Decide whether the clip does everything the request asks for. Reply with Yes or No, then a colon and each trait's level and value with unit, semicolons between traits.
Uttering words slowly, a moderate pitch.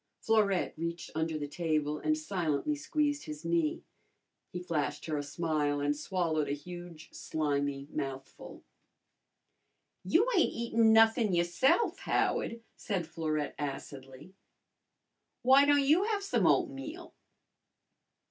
Yes: slow, 120 wpm; medium, 170 Hz